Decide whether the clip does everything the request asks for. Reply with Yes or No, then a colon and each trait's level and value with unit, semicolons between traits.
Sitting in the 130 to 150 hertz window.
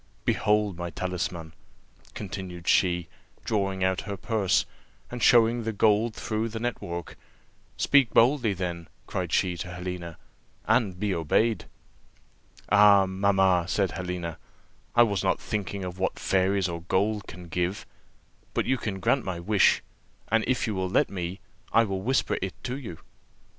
No: very low, 95 Hz